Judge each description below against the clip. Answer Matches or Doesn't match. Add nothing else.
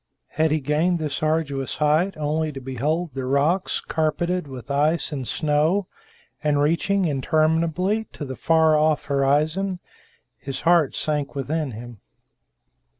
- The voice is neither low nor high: Matches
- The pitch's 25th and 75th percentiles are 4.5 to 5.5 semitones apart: Doesn't match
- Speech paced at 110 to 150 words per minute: Matches